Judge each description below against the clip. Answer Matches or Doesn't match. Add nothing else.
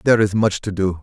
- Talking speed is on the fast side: Matches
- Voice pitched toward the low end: Matches